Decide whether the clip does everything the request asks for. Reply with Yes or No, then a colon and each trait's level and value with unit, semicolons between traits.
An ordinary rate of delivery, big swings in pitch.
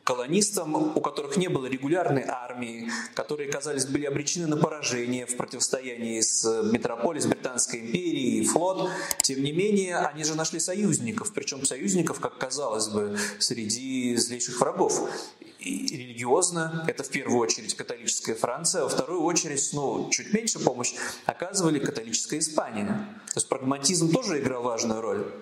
Yes: average, 150 wpm; wide, 8.8 semitones